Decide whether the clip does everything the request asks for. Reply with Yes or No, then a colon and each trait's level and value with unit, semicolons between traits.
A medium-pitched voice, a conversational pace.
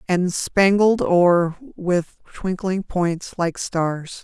No: medium, 180 Hz; slow, 115 wpm